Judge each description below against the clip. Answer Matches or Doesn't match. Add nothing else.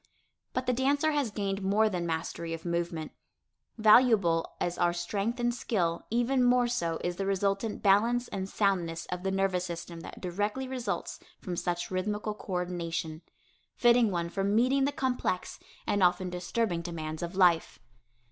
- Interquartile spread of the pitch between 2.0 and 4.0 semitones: Doesn't match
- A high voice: Matches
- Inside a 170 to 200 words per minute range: Doesn't match